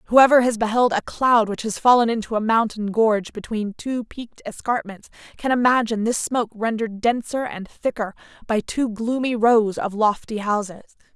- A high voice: Yes, high, 225 Hz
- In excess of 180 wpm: No, average, 165 wpm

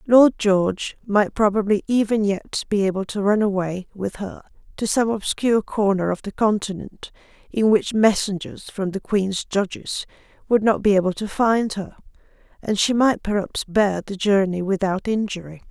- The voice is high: Yes, high, 205 Hz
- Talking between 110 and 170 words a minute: Yes, average, 165 wpm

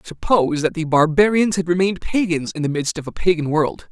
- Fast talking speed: Yes, fast, 215 wpm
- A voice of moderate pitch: Yes, medium, 170 Hz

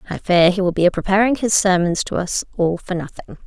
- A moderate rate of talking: No, fast, 245 wpm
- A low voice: No, medium, 185 Hz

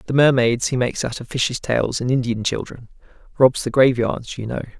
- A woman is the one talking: No, male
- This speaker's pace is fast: No, average, 190 wpm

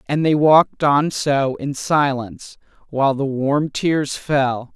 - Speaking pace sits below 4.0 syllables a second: Yes, 3.8 syllables/s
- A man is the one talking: No, female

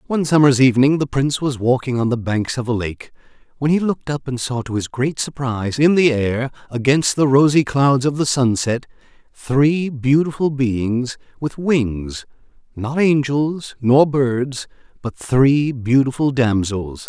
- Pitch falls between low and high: No, low, 130 Hz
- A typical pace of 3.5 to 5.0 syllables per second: Yes, 4.4 syllables/s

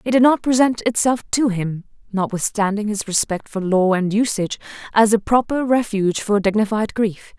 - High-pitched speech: Yes, high, 215 Hz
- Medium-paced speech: Yes, average, 170 wpm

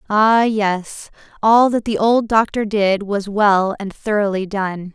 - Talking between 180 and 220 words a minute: No, average, 160 wpm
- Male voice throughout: No, female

